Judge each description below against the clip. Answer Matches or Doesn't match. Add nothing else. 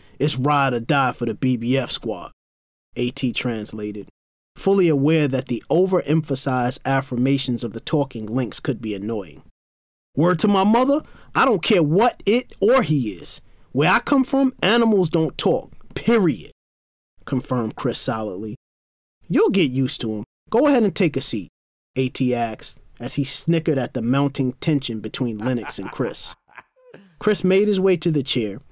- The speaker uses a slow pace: Doesn't match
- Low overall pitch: Matches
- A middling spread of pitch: Doesn't match